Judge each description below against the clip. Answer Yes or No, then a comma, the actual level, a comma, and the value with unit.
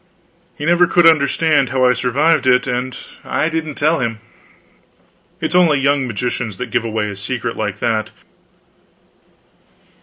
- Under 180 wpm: Yes, average, 150 wpm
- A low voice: Yes, low, 130 Hz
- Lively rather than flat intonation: No, average, 4.8 semitones